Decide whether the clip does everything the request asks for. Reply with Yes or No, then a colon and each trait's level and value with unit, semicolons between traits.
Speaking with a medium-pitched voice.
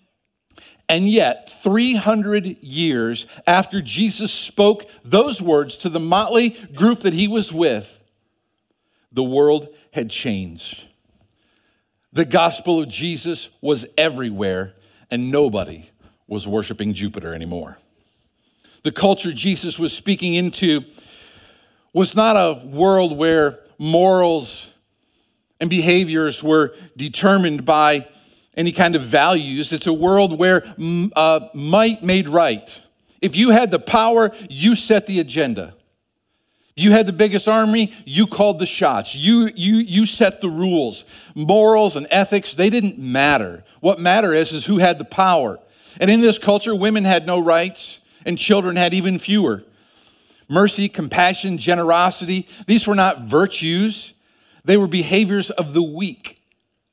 Yes: medium, 175 Hz